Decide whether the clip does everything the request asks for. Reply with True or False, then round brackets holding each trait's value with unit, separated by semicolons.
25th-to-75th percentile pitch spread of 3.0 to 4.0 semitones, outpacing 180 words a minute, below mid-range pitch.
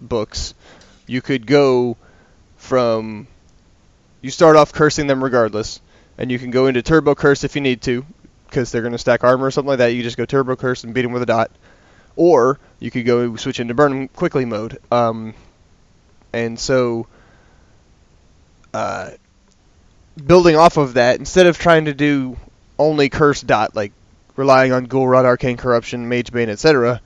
False (3.4 semitones; 175 wpm; 125 Hz)